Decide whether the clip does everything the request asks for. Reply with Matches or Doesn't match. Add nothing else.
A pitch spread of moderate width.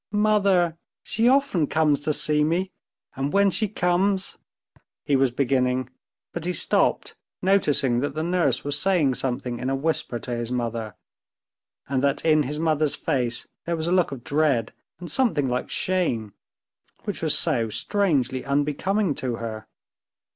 Doesn't match